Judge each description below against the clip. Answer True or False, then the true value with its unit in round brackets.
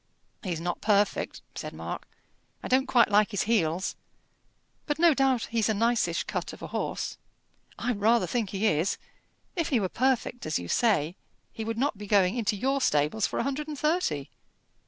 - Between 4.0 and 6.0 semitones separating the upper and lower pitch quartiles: True (5.1 semitones)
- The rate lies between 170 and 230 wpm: True (185 wpm)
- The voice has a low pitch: False (220 Hz)